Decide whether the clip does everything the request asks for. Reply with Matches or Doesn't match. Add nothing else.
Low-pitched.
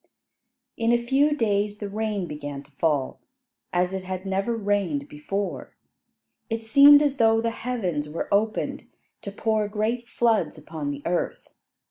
Doesn't match